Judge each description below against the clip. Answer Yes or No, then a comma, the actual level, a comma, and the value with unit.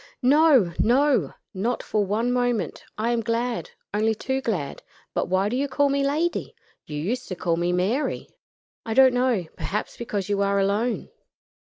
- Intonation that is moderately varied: Yes, average, 4.3 semitones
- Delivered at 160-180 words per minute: Yes, average, 170 wpm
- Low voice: No, high, 230 Hz